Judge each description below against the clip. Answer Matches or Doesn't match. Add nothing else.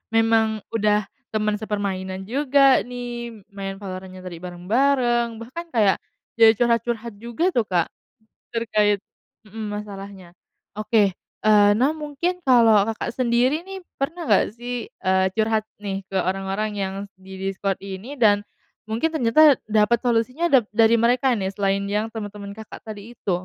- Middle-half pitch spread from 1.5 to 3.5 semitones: Matches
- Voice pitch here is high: Matches